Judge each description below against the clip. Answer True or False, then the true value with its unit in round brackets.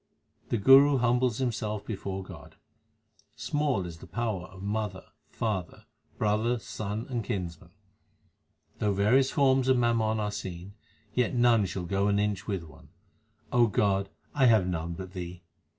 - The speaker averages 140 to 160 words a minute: True (145 wpm)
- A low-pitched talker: True (105 Hz)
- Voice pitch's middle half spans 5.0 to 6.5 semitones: False (4.0 semitones)